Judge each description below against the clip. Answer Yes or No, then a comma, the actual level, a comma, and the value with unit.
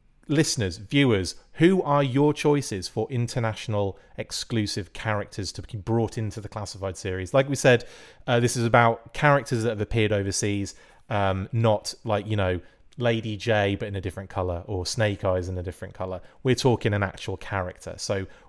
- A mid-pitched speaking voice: No, low, 105 Hz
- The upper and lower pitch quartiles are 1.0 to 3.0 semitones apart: No, average, 3.7 semitones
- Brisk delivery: No, average, 175 wpm